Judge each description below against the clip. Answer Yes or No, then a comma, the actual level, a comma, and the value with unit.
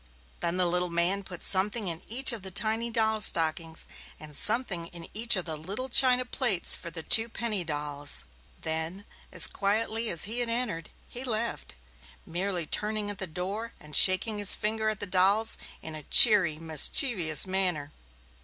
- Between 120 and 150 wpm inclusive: No, average, 170 wpm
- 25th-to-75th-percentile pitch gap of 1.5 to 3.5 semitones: No, average, 4.9 semitones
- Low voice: No, high, 195 Hz